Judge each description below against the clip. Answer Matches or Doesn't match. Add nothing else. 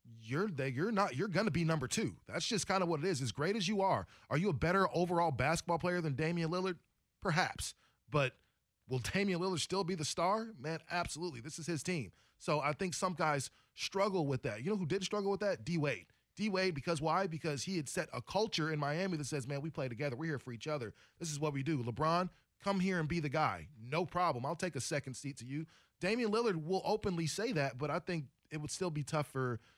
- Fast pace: Matches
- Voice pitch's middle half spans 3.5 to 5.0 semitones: Matches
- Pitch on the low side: Doesn't match